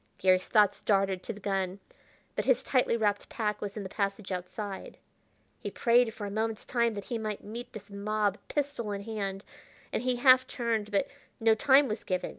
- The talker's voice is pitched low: No, high, 210 Hz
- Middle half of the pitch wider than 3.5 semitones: No, average, 2.8 semitones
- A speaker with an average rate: Yes, average, 195 wpm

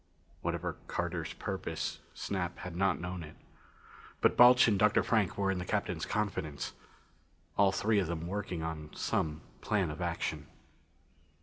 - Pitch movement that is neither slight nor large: Yes, average, 3.6 semitones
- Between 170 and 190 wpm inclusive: No, average, 145 wpm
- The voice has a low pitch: Yes, very low, 90 Hz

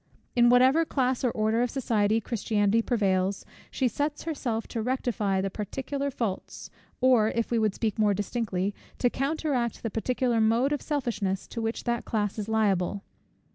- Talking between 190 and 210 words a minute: No, average, 165 wpm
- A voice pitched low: No, high, 230 Hz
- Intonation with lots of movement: No, average, 3.4 semitones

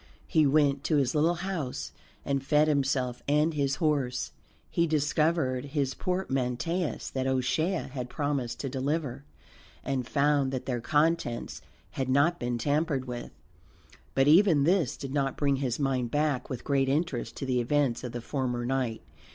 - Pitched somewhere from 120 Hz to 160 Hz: Yes, medium, 140 Hz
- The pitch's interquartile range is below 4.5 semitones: Yes, average, 3.0 semitones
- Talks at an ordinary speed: Yes, average, 160 wpm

